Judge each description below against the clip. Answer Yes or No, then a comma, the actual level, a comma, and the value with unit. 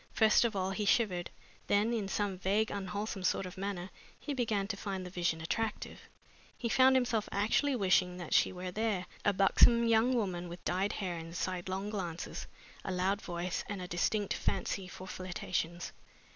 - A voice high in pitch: Yes, high, 195 Hz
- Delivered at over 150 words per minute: Yes, average, 175 wpm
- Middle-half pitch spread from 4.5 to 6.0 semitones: No, average, 2.9 semitones